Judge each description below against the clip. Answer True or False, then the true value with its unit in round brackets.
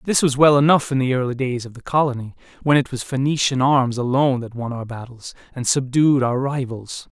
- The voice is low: True (130 Hz)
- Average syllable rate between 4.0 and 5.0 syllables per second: False (5.5 syllables/s)